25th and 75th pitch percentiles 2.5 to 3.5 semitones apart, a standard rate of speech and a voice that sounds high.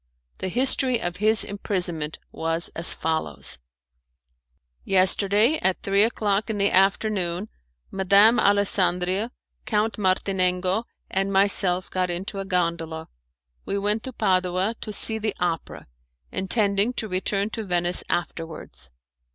No: average, 2.8 semitones; slow, 120 wpm; high, 195 Hz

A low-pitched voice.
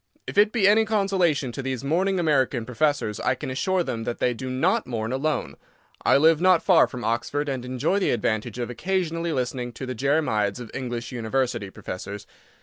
Yes: low, 130 Hz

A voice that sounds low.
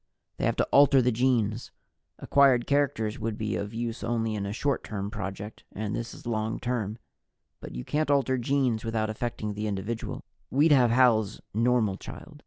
Yes: low, 115 Hz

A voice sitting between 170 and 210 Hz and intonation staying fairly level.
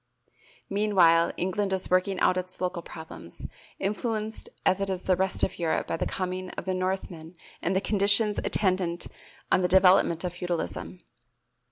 Yes: medium, 185 Hz; narrow, 1.9 semitones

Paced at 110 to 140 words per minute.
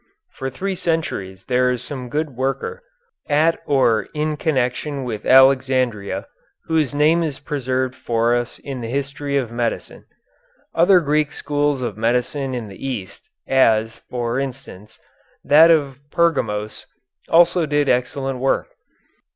Yes: slow, 135 wpm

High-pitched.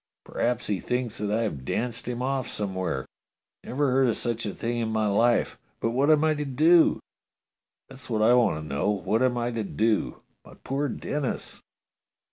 No: low, 120 Hz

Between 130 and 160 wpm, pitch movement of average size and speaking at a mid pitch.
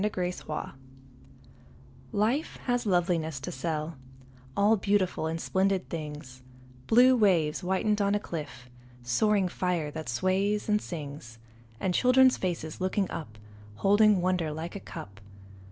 Yes: slow, 135 wpm; average, 4.8 semitones; medium, 180 Hz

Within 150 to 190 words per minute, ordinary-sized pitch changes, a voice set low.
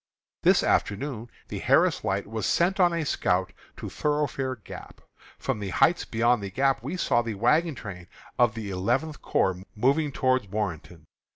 No: average, 165 wpm; wide, 6.0 semitones; low, 120 Hz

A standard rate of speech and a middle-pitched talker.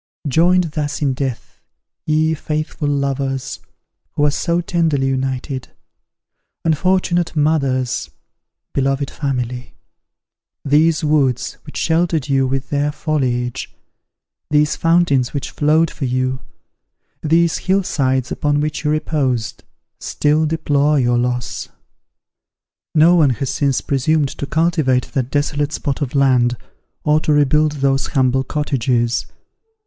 No: slow, 120 wpm; medium, 145 Hz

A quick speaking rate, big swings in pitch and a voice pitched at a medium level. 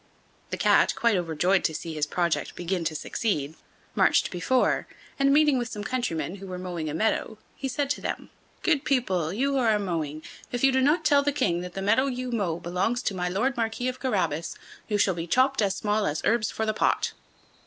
No: fast, 215 wpm; wide, 6.5 semitones; high, 210 Hz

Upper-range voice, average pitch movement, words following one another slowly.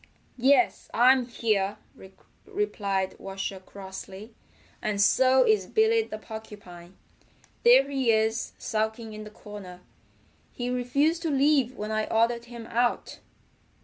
Yes: high, 225 Hz; average, 3.8 semitones; slow, 120 wpm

